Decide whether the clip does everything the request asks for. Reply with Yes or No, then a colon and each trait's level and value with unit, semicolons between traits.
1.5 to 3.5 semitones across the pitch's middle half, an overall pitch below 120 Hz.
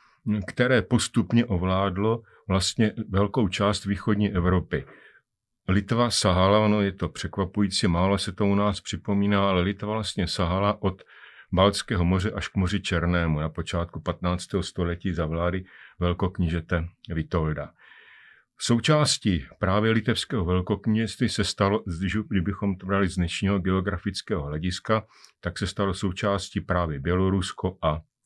Yes: average, 2.8 semitones; low, 100 Hz